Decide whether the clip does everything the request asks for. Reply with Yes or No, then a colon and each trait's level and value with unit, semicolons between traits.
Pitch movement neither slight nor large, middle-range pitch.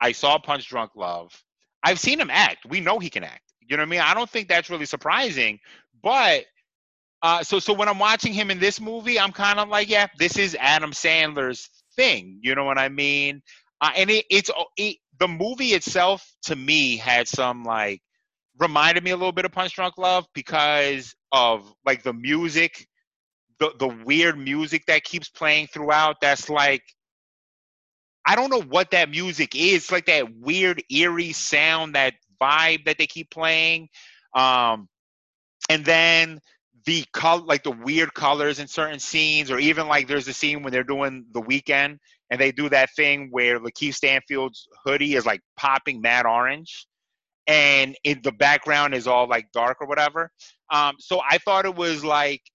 Yes: average, 4.3 semitones; medium, 150 Hz